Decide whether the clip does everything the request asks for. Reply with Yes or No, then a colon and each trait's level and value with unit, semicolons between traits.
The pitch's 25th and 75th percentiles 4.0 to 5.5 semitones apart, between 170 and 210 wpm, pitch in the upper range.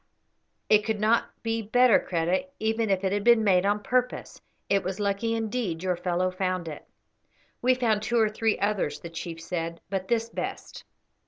No: average, 3.6 semitones; average, 180 wpm; high, 205 Hz